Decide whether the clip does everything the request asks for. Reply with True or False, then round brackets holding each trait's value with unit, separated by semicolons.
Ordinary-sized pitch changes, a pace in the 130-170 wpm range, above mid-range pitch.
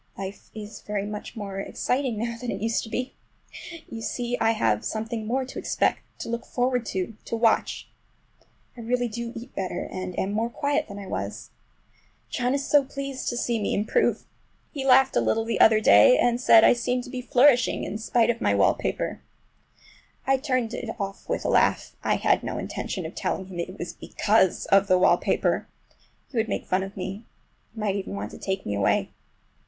False (3.8 semitones; 200 wpm; 225 Hz)